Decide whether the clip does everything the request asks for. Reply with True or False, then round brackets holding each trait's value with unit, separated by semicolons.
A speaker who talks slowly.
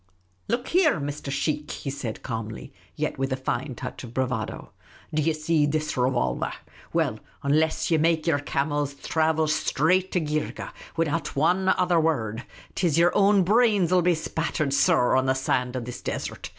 False (180 wpm)